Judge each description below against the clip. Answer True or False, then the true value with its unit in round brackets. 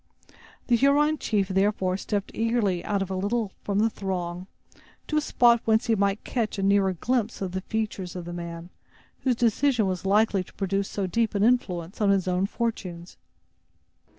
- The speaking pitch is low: False (200 Hz)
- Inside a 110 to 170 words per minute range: False (180 wpm)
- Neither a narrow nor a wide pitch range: True (3.4 semitones)